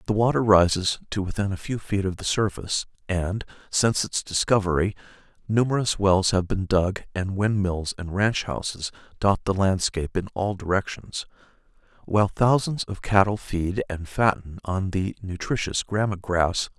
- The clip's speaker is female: No, male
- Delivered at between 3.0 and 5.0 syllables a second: Yes, 4.8 syllables/s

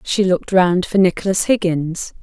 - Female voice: Yes, female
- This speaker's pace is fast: No, average, 160 wpm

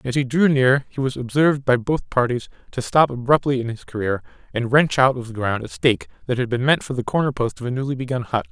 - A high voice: No, low, 125 Hz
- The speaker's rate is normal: No, fast, 260 wpm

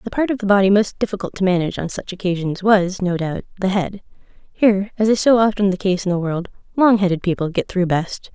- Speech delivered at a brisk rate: Yes, fast, 235 wpm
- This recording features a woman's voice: Yes, female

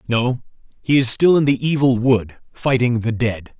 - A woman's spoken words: No, male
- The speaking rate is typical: Yes, average, 185 wpm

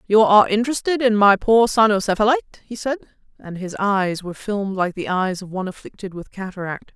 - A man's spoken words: No, female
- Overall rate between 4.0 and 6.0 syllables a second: No, 6.2 syllables/s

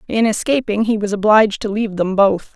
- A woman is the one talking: Yes, female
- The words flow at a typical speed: No, fast, 210 wpm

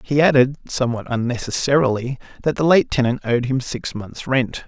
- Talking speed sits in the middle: Yes, average, 165 wpm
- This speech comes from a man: Yes, male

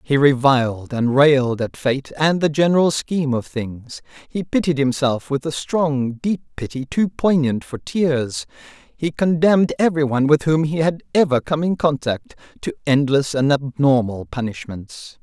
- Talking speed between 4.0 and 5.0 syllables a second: Yes, 4.6 syllables/s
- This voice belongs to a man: Yes, male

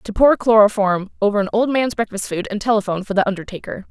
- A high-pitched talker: Yes, high, 210 Hz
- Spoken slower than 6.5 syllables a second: No, 6.6 syllables/s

